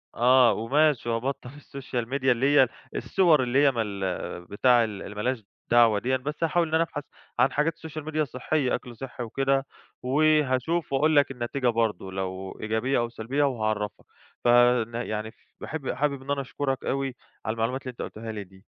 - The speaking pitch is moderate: No, low, 130 Hz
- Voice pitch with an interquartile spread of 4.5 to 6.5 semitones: No, average, 3.9 semitones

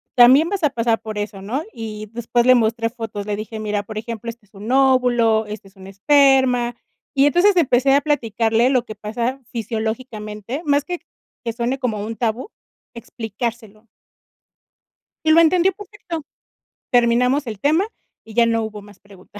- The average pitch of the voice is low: No, high, 235 Hz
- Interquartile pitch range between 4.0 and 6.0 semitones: No, average, 3.6 semitones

